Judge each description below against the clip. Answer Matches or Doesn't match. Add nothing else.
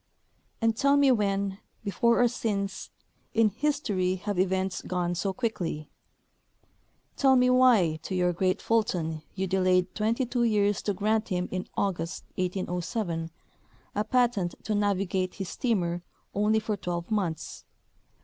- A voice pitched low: Doesn't match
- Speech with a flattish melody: Doesn't match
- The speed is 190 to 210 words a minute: Doesn't match